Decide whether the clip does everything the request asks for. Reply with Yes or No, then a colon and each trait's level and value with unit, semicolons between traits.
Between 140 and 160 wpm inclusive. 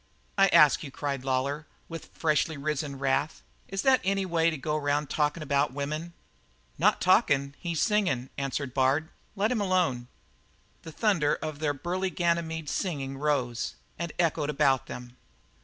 Yes: average, 155 wpm